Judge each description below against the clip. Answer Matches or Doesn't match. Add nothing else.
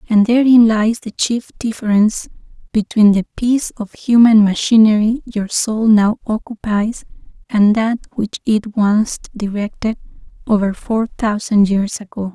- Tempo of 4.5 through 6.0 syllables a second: Doesn't match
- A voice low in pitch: Doesn't match